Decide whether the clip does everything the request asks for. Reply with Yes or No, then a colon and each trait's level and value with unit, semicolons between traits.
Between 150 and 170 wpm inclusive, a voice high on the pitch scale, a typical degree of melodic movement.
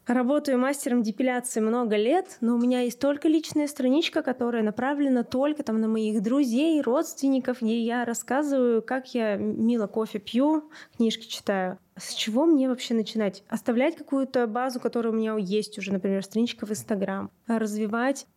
Yes: average, 155 wpm; high, 240 Hz; average, 3.4 semitones